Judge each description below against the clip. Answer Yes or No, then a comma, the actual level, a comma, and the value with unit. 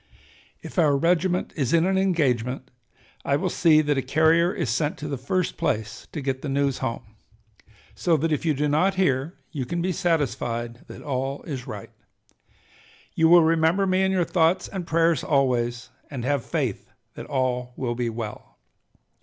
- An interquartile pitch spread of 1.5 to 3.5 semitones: No, average, 4.7 semitones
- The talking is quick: No, average, 180 wpm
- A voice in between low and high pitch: Yes, medium, 150 Hz